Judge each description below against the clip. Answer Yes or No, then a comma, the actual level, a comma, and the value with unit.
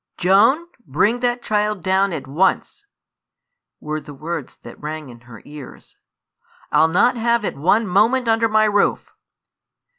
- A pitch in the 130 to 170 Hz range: No, high, 190 Hz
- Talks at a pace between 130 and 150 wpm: Yes, average, 145 wpm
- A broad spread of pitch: Yes, wide, 6.9 semitones